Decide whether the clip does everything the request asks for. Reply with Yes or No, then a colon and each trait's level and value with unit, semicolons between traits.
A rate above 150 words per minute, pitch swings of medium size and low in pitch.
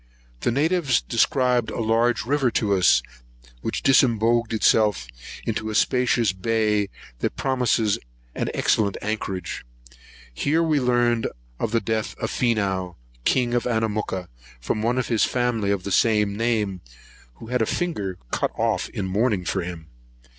No: average, 145 wpm; average, 3.4 semitones; low, 110 Hz